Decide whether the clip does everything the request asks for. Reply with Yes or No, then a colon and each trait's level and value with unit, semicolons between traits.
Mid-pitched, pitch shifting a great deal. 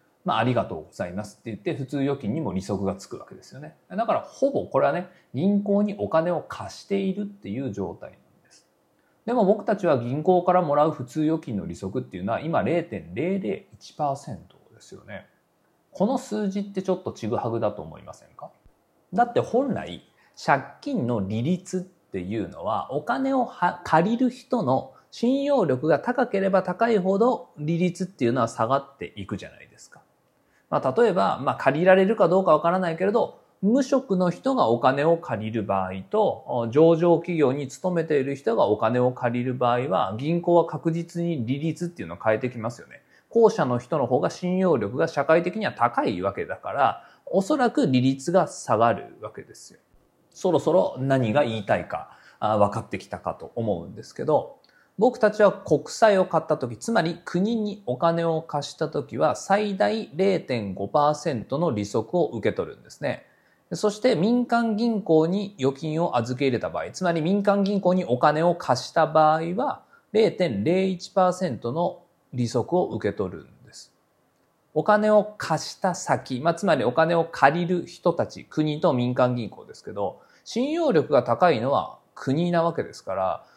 Yes: medium, 170 Hz; wide, 7.3 semitones